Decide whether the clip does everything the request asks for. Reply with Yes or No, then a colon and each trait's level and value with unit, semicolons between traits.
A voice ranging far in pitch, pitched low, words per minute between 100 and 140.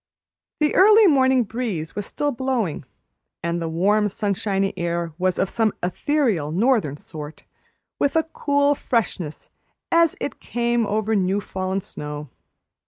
No: wide, 7.1 semitones; high, 205 Hz; slow, 135 wpm